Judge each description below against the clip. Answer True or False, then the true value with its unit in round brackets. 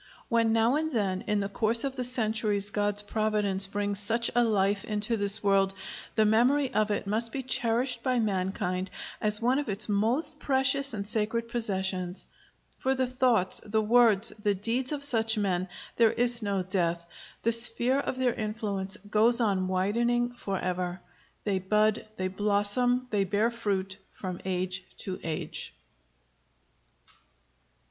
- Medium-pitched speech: False (215 Hz)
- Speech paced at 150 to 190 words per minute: True (155 wpm)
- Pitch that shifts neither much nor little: True (3.3 semitones)